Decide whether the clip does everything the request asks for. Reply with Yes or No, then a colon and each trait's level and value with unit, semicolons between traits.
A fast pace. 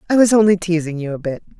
Yes: fast, 265 wpm